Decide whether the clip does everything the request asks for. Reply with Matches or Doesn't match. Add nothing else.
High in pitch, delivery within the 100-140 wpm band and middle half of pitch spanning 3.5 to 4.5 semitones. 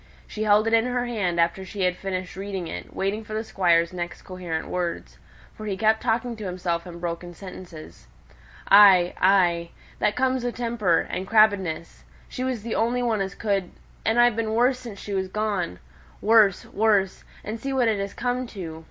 Doesn't match